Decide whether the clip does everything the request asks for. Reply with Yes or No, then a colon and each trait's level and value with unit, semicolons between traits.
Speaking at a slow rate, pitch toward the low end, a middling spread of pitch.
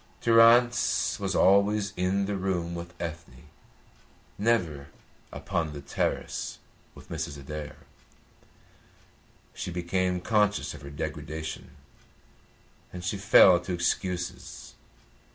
Yes: slow, 100 wpm; very low, 90 Hz; average, 3.5 semitones